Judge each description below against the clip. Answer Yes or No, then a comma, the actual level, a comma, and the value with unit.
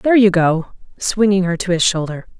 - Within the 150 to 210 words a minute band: Yes, average, 200 wpm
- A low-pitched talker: No, high, 190 Hz